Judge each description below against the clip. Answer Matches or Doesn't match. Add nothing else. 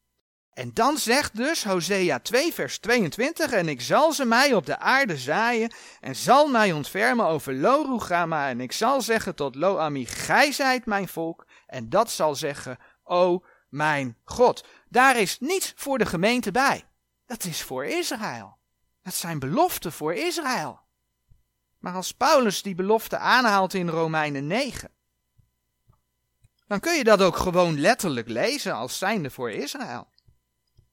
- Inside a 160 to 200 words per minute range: Doesn't match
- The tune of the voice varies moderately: Doesn't match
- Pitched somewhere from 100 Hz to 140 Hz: Doesn't match